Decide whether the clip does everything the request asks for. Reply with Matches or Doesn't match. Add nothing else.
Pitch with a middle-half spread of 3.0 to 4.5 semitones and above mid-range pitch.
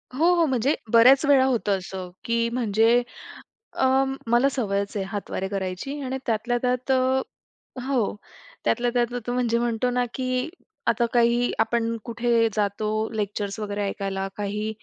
Matches